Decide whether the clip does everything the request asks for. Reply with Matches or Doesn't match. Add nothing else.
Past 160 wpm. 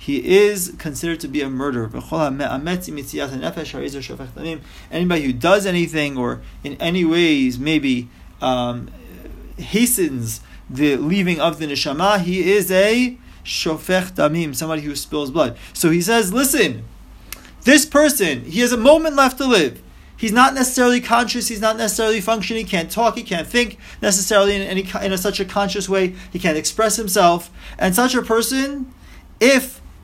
Doesn't match